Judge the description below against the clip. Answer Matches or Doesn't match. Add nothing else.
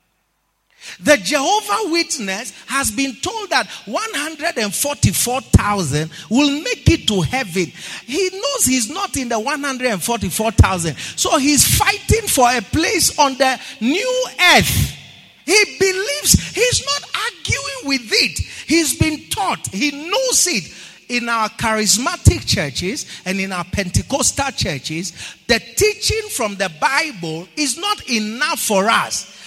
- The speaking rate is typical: Doesn't match